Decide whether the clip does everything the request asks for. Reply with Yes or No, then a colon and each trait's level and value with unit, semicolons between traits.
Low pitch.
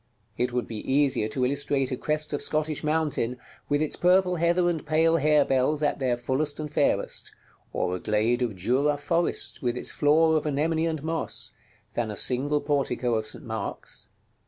No: medium, 145 Hz